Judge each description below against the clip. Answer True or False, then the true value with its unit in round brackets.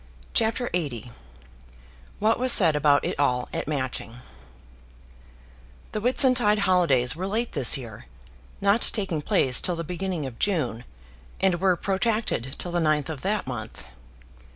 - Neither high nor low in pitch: True (170 Hz)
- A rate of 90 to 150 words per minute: True (140 wpm)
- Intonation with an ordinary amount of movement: False (7.1 semitones)